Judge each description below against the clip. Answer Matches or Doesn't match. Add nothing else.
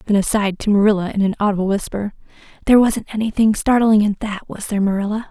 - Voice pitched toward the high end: Matches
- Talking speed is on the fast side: Doesn't match